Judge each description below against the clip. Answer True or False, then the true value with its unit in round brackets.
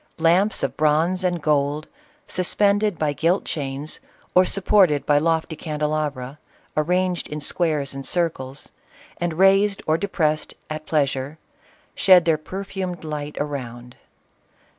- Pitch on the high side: False (155 Hz)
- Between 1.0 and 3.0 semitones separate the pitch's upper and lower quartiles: False (3.6 semitones)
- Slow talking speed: True (125 wpm)